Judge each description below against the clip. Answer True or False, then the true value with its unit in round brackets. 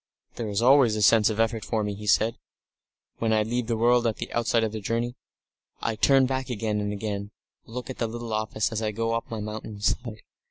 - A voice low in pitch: True (110 Hz)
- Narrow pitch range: True (1.7 semitones)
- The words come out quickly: True (235 wpm)